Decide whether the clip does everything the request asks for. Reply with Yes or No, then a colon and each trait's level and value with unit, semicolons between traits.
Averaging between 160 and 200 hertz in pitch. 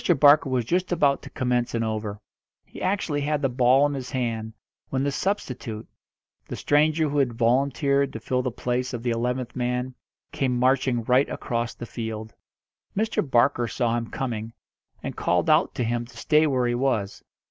No: low, 125 Hz